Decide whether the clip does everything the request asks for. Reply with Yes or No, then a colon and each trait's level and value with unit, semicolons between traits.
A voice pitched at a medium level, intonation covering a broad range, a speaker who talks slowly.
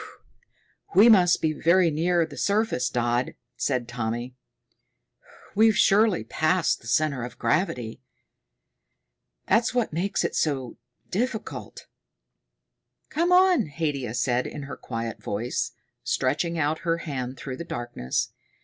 Yes: medium, 155 Hz; wide, 7.0 semitones; slow, 120 wpm